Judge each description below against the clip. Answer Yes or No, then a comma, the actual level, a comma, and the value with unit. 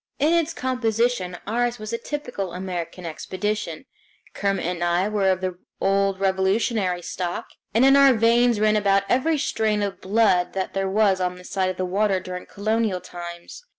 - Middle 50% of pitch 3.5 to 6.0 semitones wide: Yes, average, 3.8 semitones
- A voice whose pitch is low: No, high, 195 Hz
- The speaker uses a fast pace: No, average, 175 wpm